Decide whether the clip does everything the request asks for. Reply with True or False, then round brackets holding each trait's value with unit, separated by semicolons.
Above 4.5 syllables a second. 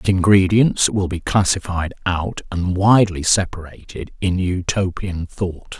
False (4.2 syllables/s)